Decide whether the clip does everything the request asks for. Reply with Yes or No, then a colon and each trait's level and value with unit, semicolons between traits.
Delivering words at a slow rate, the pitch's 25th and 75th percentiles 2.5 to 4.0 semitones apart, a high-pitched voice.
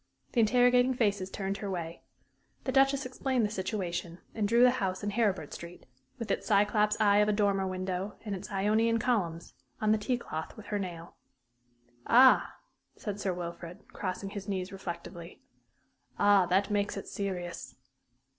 No: average, 165 wpm; average, 2.9 semitones; high, 205 Hz